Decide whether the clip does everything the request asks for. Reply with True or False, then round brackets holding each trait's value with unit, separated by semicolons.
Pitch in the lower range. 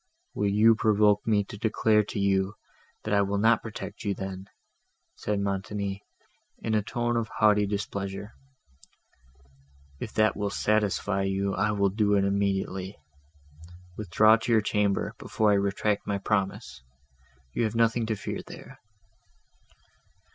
True (105 Hz)